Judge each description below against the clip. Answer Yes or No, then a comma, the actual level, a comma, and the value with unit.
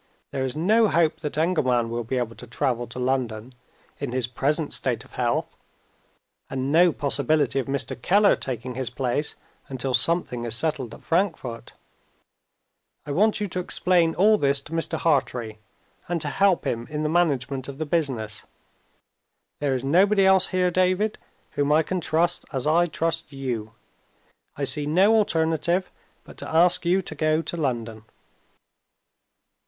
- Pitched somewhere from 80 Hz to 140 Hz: No, medium, 150 Hz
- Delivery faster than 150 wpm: Yes, average, 160 wpm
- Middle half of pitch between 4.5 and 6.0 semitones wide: Yes, average, 5.2 semitones